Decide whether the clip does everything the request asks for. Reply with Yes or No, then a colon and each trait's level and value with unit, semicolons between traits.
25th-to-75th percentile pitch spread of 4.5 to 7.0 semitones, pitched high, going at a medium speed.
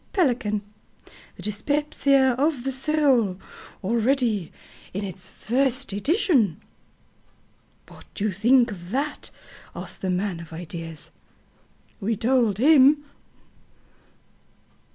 No: wide, 5.6 semitones; high, 235 Hz; slow, 100 wpm